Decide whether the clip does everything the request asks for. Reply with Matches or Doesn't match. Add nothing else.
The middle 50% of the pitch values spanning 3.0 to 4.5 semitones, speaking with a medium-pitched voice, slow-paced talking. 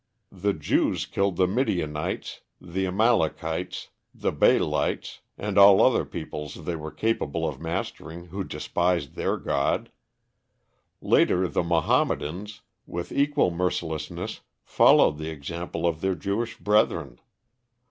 Doesn't match